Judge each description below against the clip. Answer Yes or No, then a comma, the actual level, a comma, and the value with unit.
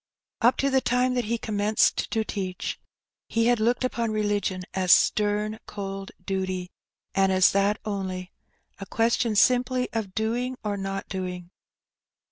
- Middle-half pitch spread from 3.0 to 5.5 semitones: Yes, average, 3.3 semitones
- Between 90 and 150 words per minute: Yes, average, 145 wpm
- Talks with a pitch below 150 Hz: No, high, 210 Hz